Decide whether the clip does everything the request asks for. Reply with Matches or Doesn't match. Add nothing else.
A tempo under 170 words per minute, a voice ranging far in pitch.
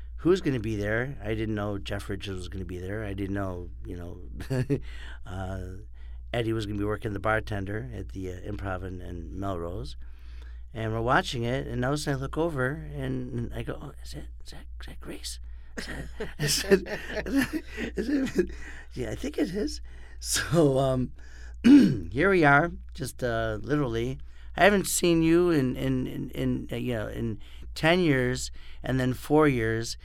Doesn't match